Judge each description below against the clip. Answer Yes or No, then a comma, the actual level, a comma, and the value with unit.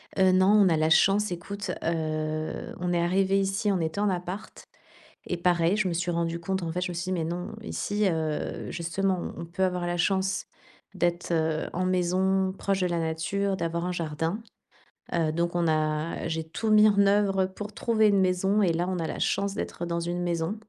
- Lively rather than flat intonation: No, narrow, 2.5 semitones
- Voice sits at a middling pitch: Yes, medium, 180 Hz